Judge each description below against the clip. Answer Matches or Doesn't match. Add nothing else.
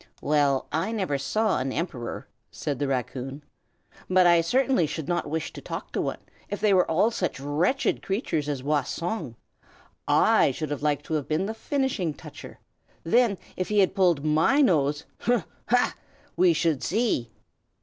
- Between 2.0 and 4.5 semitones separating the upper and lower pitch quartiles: Doesn't match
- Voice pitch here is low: Doesn't match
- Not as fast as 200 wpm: Matches